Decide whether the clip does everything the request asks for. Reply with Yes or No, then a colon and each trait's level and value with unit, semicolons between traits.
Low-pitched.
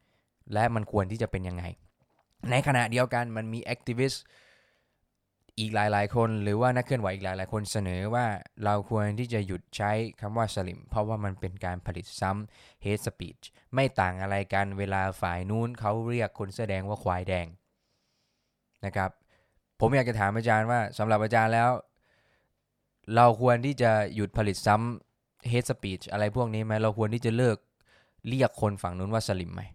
Yes: low, 105 Hz